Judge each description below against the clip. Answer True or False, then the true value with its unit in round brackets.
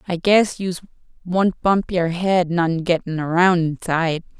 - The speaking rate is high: False (150 wpm)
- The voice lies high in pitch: False (175 Hz)